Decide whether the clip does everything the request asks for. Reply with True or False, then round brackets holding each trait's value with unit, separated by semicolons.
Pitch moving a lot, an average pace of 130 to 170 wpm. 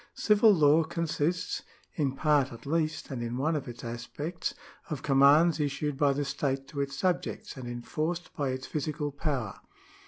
False (2.7 semitones; 165 wpm)